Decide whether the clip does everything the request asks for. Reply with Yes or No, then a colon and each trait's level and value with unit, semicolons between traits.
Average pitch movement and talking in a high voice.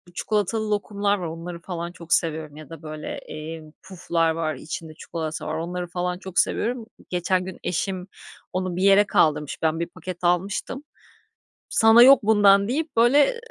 No: average, 3.9 semitones; medium, 180 Hz